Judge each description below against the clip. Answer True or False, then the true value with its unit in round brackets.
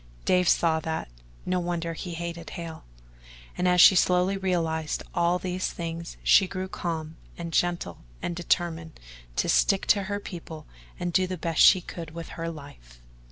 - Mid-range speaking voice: True (170 Hz)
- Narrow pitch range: True (1.8 semitones)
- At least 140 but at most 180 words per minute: True (165 wpm)